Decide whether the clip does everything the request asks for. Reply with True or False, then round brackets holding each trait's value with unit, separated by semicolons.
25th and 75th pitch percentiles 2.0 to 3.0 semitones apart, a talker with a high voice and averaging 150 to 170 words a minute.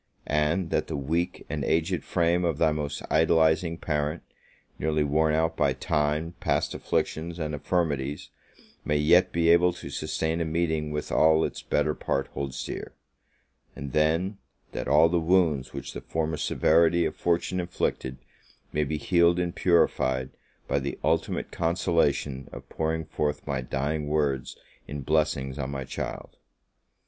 False (2.5 semitones; 80 Hz; 155 wpm)